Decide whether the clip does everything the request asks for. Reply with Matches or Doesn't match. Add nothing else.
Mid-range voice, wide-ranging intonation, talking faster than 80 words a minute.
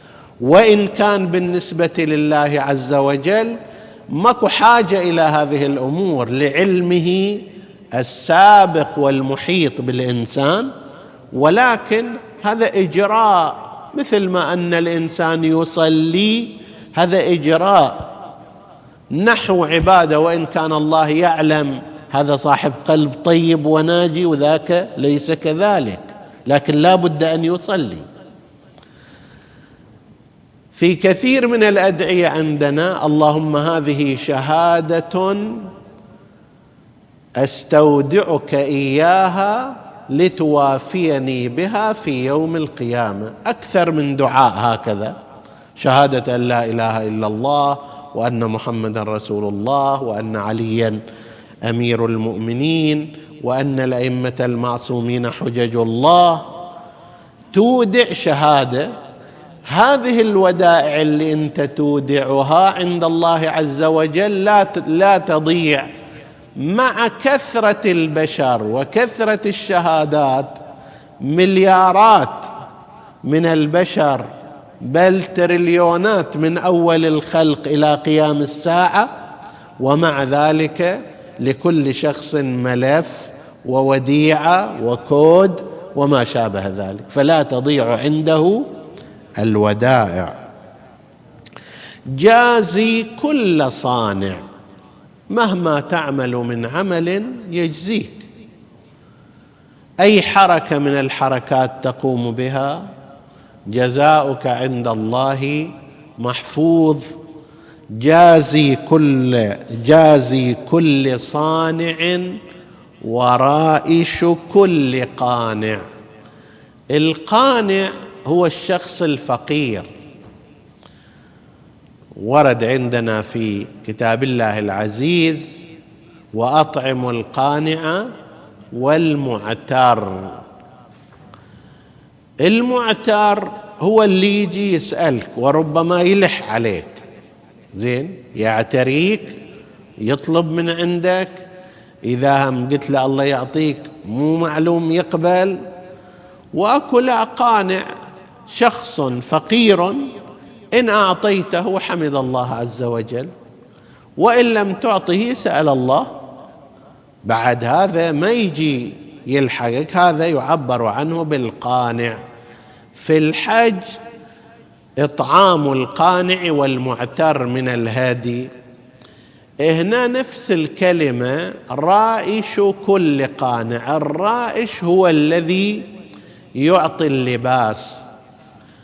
Doesn't match